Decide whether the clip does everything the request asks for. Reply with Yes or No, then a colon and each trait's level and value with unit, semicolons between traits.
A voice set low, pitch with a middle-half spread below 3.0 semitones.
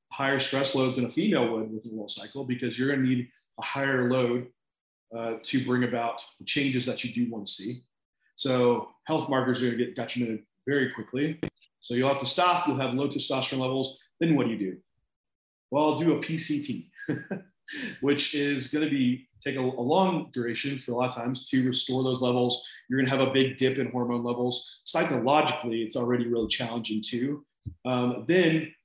Yes: low, 130 Hz; narrow, 2.4 semitones